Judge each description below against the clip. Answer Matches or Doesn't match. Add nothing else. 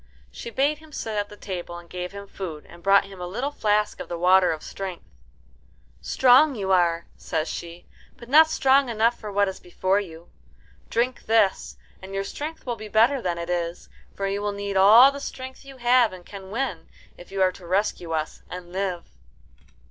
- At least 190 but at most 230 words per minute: Matches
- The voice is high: Matches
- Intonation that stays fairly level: Doesn't match